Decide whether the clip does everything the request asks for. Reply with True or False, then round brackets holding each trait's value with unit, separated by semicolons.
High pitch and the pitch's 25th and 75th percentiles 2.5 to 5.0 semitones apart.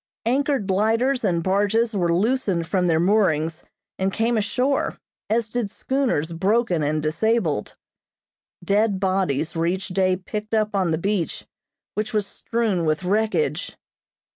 True (200 Hz; 4.5 semitones)